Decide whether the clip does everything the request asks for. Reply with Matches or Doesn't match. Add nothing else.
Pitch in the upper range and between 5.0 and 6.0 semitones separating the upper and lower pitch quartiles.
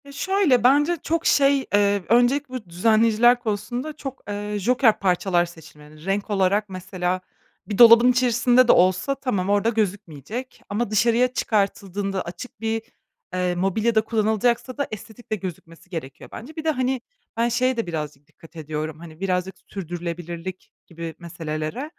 Matches